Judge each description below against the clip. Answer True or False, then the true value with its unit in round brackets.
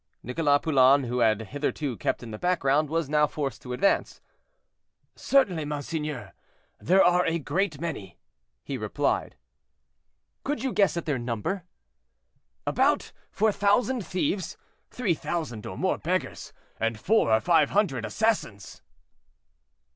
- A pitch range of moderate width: False (6.6 semitones)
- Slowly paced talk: True (130 wpm)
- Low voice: False (150 Hz)